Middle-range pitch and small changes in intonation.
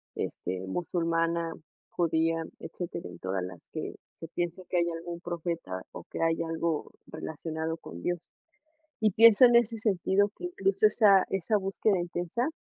No: medium, 170 Hz; average, 3.1 semitones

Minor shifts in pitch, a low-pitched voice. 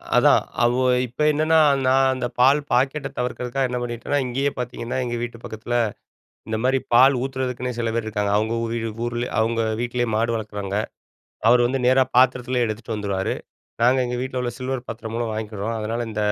Yes: narrow, 2.2 semitones; low, 120 Hz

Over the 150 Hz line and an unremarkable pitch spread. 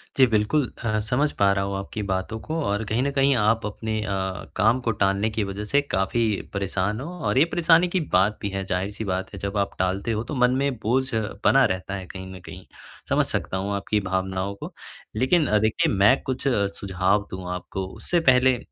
No: low, 105 Hz; average, 4.4 semitones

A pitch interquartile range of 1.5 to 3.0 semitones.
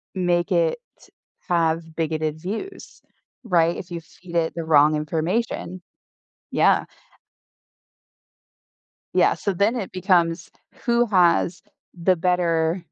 Yes: narrow, 2.5 semitones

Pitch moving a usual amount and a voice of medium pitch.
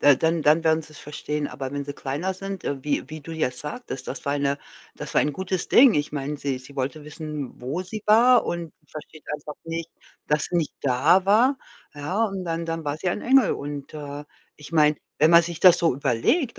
Yes: average, 3.3 semitones; medium, 155 Hz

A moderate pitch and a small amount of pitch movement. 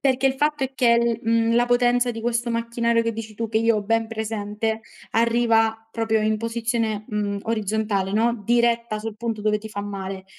No: high, 225 Hz; narrow, 1.5 semitones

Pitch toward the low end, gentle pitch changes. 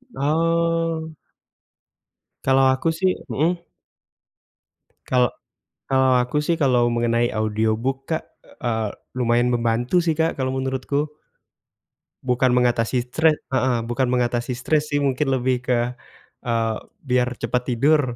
No: low, 130 Hz; average, 3.6 semitones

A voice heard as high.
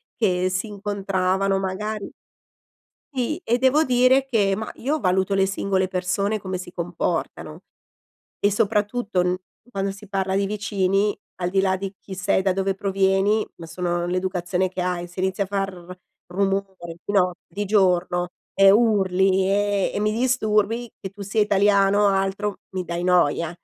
Yes: high, 195 Hz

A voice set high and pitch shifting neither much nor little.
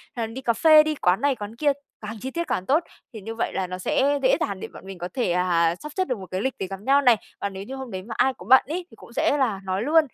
No: high, 230 Hz; wide, 6.4 semitones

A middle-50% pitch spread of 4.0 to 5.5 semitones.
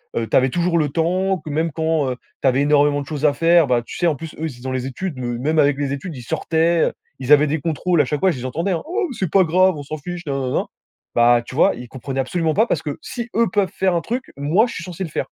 Yes: average, 4.3 semitones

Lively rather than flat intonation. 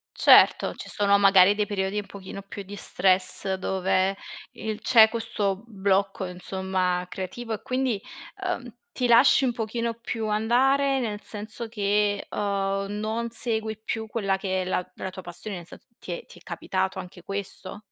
No: average, 2.8 semitones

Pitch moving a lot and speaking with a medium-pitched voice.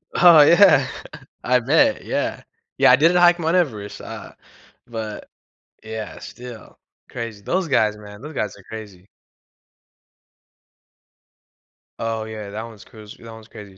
No: wide, 5.7 semitones; low, 115 Hz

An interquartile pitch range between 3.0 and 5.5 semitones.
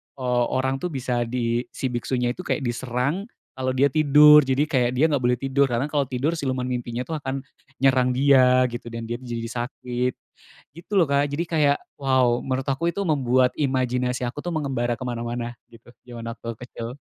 No: narrow, 2.5 semitones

